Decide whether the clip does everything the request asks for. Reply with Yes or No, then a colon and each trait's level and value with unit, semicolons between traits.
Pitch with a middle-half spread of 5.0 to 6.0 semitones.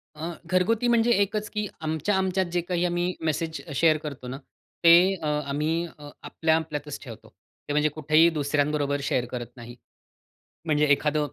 No: average, 3.3 semitones